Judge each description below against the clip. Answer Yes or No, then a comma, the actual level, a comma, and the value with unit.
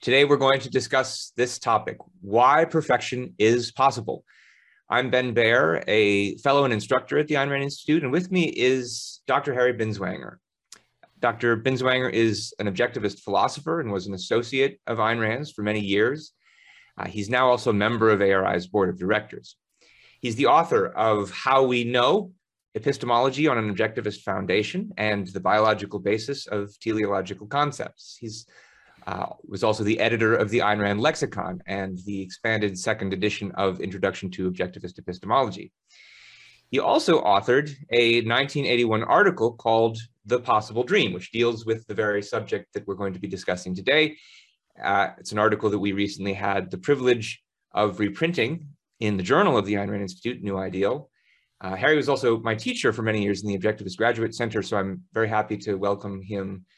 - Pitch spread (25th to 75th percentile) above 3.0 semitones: Yes, average, 4.4 semitones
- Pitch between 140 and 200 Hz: No, low, 115 Hz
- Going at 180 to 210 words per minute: No, average, 170 wpm